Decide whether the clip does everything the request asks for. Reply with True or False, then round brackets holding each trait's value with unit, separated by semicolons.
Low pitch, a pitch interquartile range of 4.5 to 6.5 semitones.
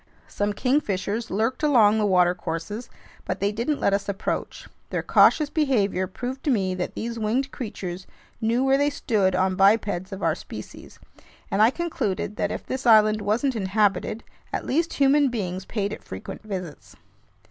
False (215 Hz; 4.8 semitones)